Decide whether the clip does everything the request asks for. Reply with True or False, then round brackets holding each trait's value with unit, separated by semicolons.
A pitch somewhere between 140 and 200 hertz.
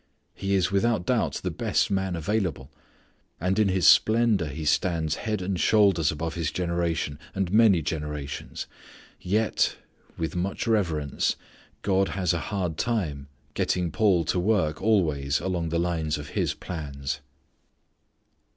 False (90 Hz)